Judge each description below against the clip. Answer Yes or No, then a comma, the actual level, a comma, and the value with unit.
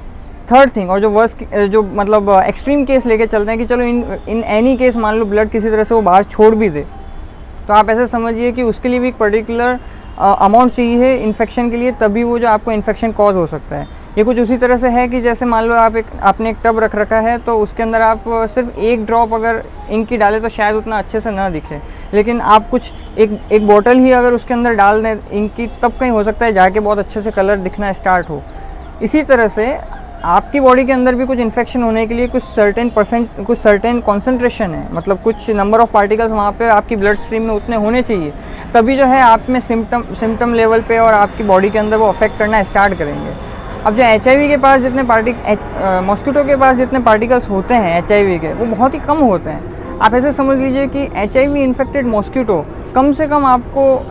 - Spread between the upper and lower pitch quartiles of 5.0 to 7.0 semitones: No, average, 2.7 semitones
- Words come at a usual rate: No, fast, 225 wpm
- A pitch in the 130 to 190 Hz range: No, high, 225 Hz